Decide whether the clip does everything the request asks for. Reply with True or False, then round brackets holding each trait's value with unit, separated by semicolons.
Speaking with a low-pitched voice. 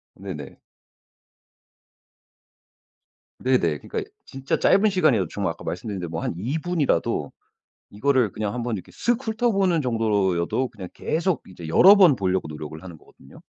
True (110 Hz)